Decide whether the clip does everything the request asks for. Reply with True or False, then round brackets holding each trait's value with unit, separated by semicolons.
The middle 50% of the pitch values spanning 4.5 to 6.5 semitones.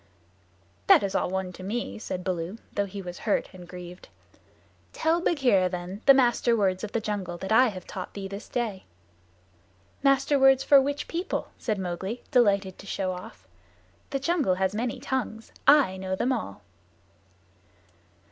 True (5.4 semitones)